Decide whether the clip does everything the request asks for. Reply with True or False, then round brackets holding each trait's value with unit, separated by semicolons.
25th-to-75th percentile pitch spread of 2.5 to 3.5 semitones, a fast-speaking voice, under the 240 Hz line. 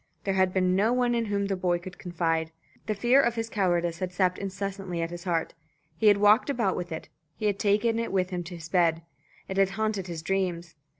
True (2.8 semitones; 225 wpm; 190 Hz)